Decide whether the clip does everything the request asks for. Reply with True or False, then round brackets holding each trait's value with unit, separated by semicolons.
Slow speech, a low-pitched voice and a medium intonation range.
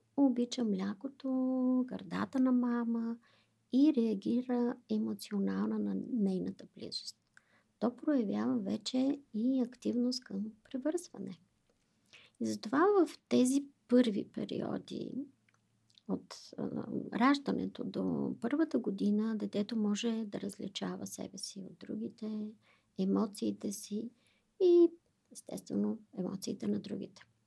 False (95 wpm; 230 Hz; 3.7 semitones)